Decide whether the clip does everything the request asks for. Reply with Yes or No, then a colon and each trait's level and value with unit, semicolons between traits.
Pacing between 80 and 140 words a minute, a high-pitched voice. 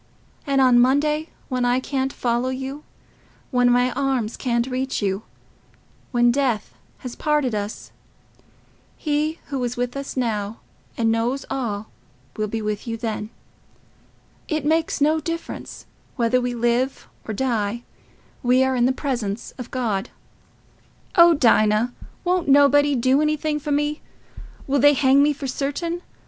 Yes: slow, 135 wpm; very high, 255 Hz